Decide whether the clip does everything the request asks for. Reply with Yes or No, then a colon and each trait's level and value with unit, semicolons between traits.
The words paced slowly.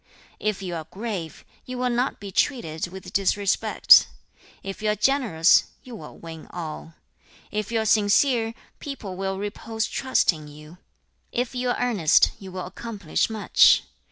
No: average, 155 wpm